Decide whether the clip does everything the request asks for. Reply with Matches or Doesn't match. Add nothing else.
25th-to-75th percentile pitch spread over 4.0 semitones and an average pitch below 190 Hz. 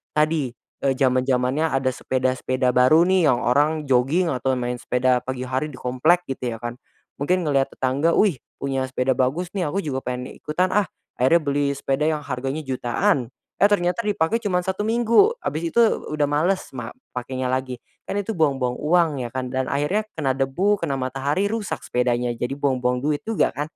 Matches